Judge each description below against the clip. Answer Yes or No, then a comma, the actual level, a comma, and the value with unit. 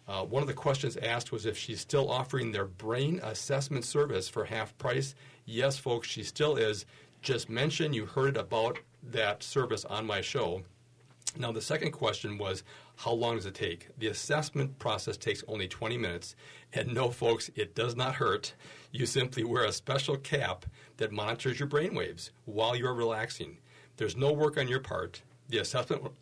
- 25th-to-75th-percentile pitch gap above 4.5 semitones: No, average, 3.9 semitones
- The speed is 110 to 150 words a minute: No, average, 180 wpm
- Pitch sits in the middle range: No, low, 125 Hz